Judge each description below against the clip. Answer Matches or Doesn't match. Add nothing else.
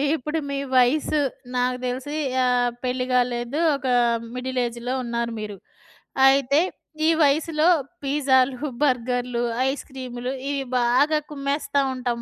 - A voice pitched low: Doesn't match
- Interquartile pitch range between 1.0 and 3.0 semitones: Matches